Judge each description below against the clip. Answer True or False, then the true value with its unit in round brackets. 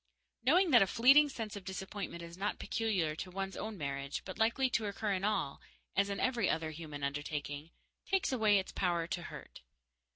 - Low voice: False (195 Hz)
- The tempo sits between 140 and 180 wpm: False (190 wpm)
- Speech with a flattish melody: False (5.2 semitones)